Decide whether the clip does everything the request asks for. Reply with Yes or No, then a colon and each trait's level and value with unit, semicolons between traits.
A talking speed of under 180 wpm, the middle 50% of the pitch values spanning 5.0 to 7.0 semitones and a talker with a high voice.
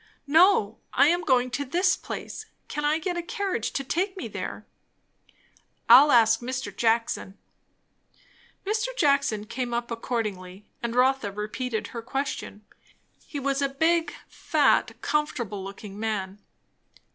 Yes: slow, 135 wpm; wide, 5.4 semitones; very high, 255 Hz